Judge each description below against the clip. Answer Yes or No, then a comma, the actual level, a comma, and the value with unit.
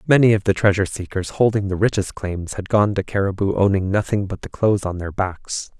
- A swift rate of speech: Yes, fast, 215 wpm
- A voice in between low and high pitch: No, low, 100 Hz